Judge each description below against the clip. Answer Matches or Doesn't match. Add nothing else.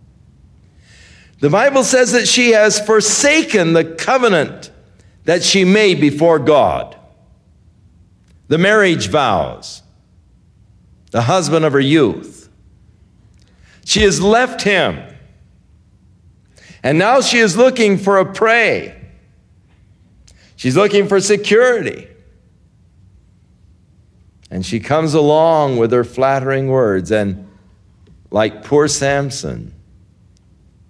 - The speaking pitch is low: Matches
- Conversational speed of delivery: Doesn't match